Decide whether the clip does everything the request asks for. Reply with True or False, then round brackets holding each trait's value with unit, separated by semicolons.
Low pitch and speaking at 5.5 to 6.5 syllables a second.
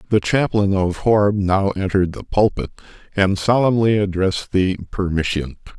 False (100 Hz; 4.9 syllables/s)